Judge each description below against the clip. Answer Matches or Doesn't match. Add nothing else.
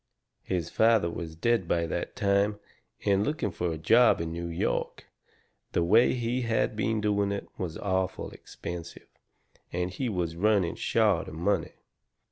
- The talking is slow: Doesn't match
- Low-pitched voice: Matches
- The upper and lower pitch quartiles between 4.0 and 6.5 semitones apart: Matches